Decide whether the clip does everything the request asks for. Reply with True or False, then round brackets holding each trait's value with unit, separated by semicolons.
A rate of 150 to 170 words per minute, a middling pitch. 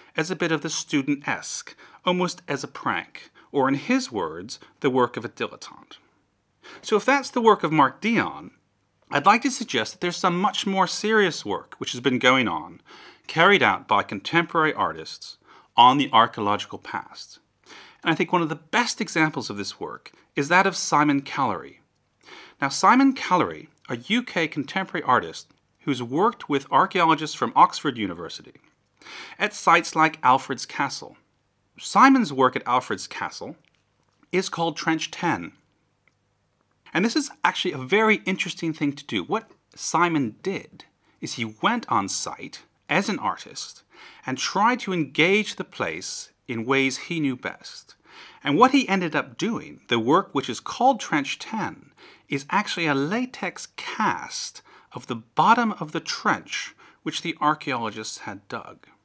True (160 wpm; 165 Hz)